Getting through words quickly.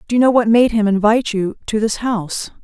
Yes: fast, 250 wpm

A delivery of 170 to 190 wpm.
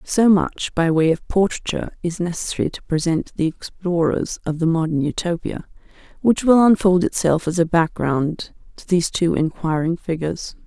No: average, 160 wpm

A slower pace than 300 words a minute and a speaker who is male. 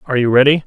Yes: fast, 270 wpm; male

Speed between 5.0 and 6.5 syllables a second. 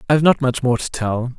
Yes: 5.8 syllables/s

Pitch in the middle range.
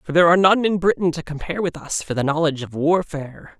Yes: medium, 165 Hz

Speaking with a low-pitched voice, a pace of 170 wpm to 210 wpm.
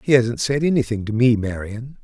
Yes: low, 120 Hz; fast, 205 wpm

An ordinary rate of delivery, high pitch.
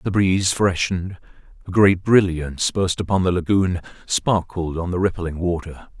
No: average, 150 wpm; very low, 90 Hz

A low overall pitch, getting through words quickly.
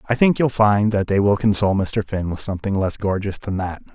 Yes: low, 100 Hz; fast, 245 wpm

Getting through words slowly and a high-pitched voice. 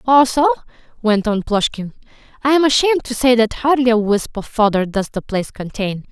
No: average, 185 wpm; high, 230 Hz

